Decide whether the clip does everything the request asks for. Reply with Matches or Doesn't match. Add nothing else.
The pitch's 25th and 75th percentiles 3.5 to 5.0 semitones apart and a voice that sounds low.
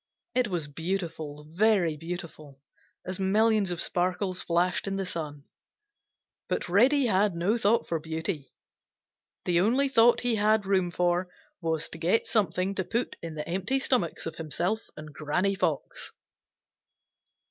Doesn't match